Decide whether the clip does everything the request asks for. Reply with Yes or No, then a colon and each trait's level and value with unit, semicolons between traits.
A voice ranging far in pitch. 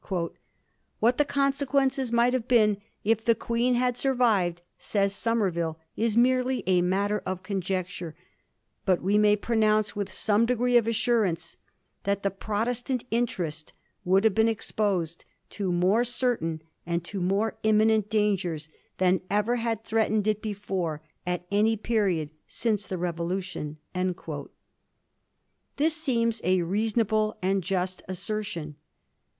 No: average, 3.9 semitones